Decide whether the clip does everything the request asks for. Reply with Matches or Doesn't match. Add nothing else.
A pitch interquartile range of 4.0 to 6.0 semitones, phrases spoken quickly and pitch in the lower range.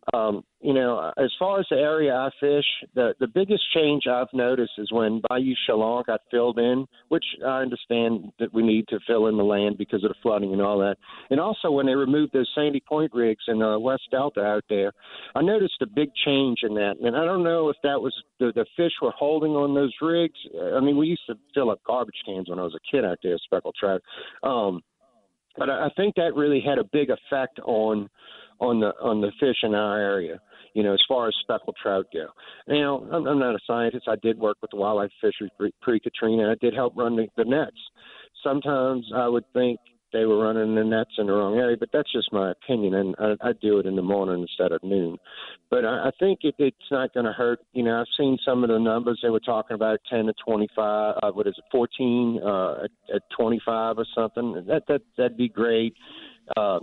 Matches